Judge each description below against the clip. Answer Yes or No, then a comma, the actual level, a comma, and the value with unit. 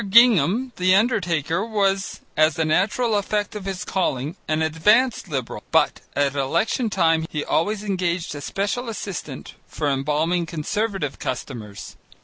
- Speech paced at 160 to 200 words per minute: No, slow, 135 wpm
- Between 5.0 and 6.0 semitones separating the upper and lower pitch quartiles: Yes, average, 5.3 semitones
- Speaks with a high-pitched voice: No, medium, 180 Hz